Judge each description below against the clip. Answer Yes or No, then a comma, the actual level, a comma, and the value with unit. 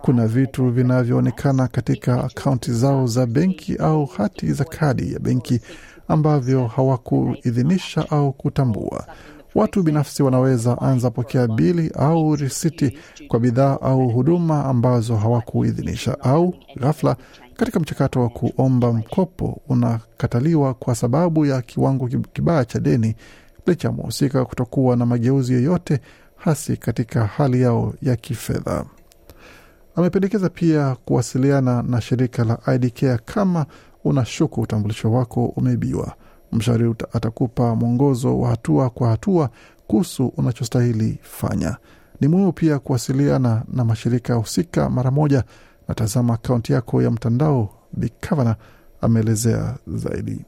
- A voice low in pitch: Yes, low, 130 Hz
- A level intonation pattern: No, average, 3.0 semitones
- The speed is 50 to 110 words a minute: No, average, 120 wpm